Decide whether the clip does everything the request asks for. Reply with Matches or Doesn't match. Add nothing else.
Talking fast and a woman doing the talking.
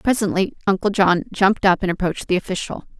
Doesn't match